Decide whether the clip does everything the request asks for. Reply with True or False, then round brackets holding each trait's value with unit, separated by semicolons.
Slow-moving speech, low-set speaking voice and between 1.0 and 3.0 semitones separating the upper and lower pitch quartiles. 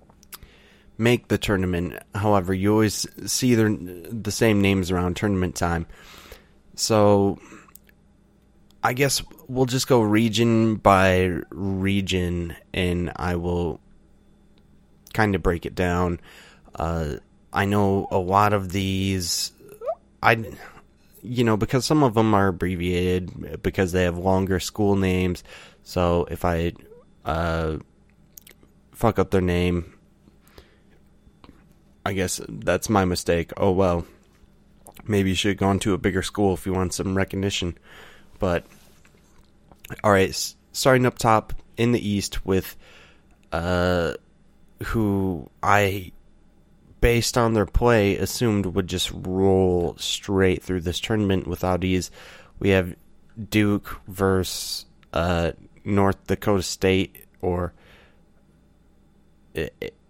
True (115 wpm; 95 Hz; 2.7 semitones)